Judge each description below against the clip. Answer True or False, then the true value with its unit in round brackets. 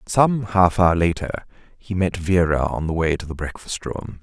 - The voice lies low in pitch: True (90 Hz)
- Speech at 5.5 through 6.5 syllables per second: False (4.5 syllables/s)